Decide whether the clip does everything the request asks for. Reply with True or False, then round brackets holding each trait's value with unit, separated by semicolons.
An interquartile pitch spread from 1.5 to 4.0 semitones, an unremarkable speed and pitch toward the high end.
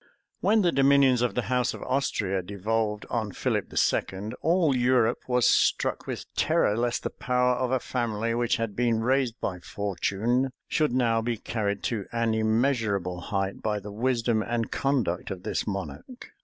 False (3.4 semitones; 170 wpm; 115 Hz)